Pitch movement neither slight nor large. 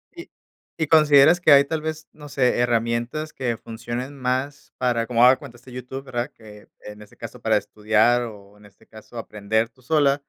Yes: average, 3.9 semitones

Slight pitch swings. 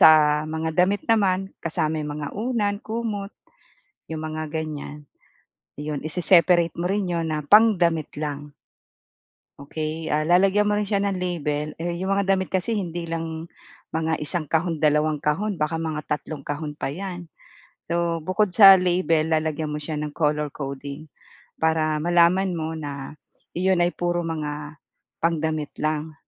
No: average, 3.2 semitones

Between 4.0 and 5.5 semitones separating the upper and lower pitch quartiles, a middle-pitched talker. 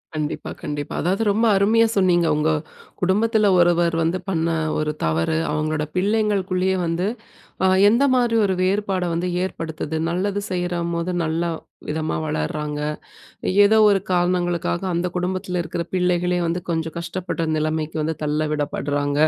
No: average, 3.1 semitones; medium, 175 Hz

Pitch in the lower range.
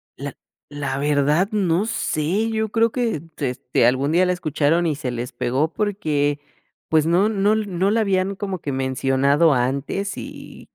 No: medium, 160 Hz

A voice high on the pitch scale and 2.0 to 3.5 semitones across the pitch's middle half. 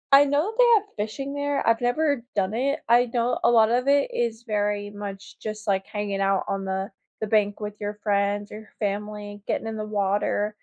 Yes: high, 215 Hz; average, 2.9 semitones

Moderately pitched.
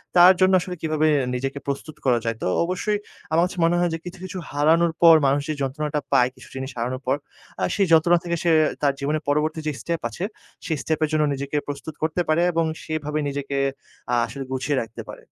Yes: medium, 155 Hz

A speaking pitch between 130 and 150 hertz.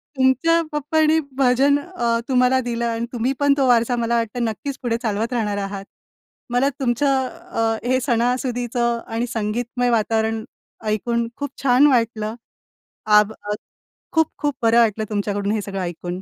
No: high, 235 Hz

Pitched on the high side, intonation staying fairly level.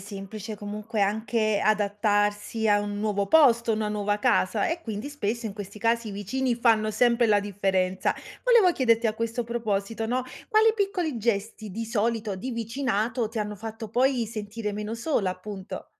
Yes: high, 220 Hz; narrow, 2.3 semitones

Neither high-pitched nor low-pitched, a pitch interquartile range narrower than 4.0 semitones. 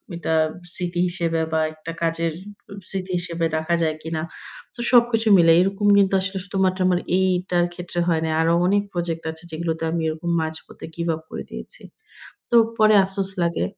Yes: medium, 175 Hz; narrow, 2.6 semitones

